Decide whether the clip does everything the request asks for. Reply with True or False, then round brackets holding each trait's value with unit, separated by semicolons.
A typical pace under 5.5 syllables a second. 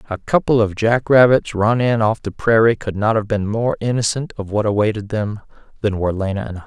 False (5.7 syllables/s)